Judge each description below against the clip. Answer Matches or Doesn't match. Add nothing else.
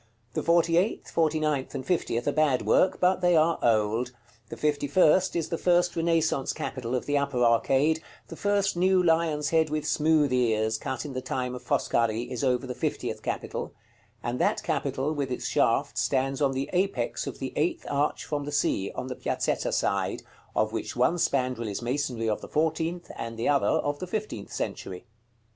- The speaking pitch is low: Doesn't match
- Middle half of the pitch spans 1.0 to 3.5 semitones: Doesn't match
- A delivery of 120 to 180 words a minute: Doesn't match